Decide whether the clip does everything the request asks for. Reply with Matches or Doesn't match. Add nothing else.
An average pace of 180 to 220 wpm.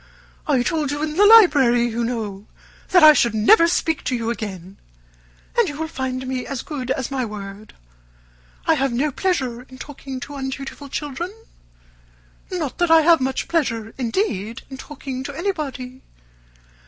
Doesn't match